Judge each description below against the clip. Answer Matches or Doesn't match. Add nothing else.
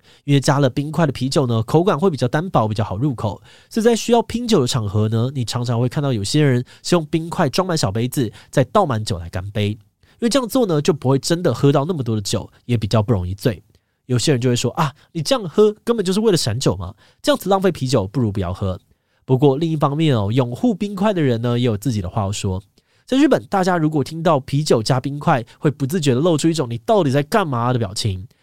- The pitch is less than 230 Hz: Matches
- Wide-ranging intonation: Matches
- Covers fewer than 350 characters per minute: Doesn't match